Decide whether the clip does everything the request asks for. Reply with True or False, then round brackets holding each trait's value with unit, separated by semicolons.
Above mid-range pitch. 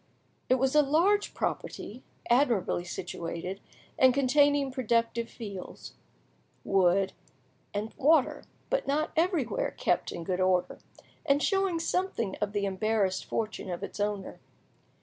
True (230 Hz)